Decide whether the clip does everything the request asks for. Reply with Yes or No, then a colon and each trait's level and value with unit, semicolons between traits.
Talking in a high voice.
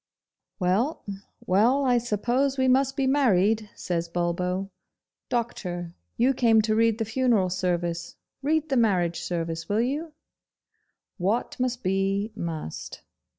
Yes: high, 215 Hz